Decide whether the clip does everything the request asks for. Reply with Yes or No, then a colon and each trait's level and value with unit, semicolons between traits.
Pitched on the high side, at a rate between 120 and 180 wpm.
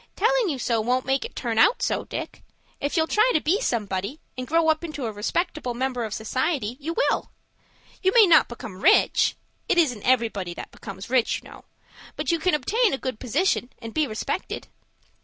No: very high, 265 Hz; average, 190 wpm